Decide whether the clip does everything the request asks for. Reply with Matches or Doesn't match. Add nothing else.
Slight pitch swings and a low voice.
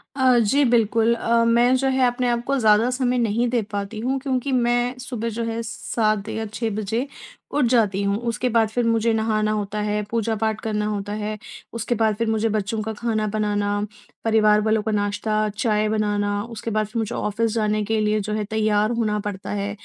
Doesn't match